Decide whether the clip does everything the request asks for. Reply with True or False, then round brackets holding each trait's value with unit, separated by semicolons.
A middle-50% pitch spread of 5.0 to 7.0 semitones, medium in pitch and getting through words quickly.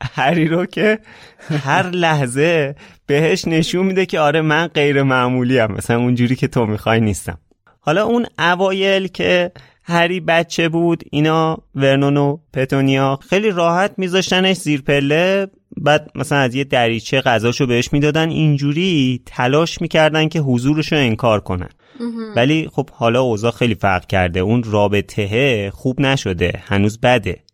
False (5.5 semitones; 145 Hz; 140 wpm)